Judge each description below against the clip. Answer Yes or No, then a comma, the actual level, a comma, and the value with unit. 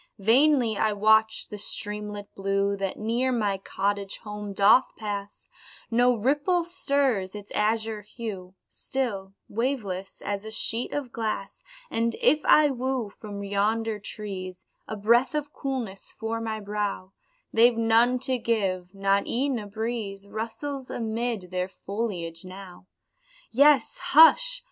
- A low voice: No, high, 220 Hz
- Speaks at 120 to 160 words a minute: Yes, slow, 135 wpm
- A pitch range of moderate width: Yes, average, 3.4 semitones